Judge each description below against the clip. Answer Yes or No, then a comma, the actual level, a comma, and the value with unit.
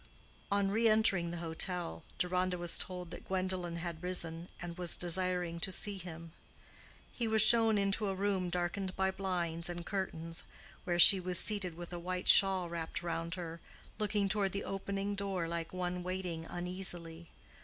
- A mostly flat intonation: Yes, narrow, 2.2 semitones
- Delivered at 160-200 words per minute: Yes, average, 165 wpm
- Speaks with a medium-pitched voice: Yes, medium, 180 Hz